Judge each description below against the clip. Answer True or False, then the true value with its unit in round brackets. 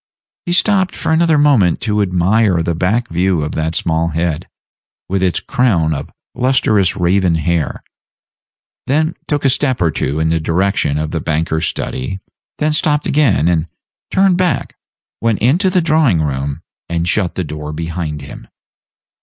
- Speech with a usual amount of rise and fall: False (8.5 semitones)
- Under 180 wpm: True (160 wpm)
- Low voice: True (90 Hz)